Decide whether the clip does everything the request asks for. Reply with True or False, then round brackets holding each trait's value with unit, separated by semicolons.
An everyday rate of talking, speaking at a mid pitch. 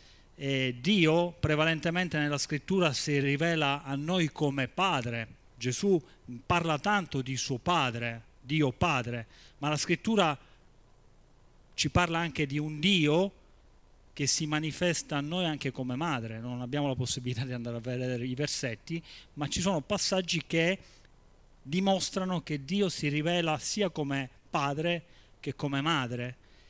True (140 wpm; 150 Hz)